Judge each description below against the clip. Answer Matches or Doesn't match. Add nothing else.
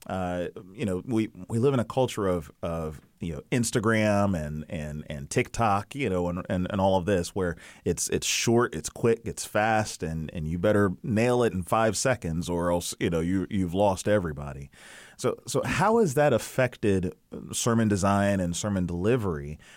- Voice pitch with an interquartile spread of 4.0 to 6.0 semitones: Matches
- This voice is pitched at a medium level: Doesn't match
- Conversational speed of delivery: Matches